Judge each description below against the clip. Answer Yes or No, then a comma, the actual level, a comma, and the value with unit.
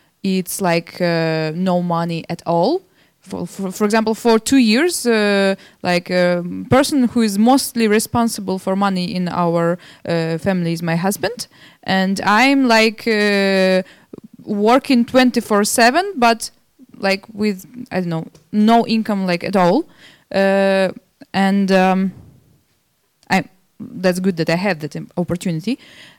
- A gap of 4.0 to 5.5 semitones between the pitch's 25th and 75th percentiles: Yes, average, 4.4 semitones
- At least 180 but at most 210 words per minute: No, average, 140 wpm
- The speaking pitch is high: Yes, high, 195 Hz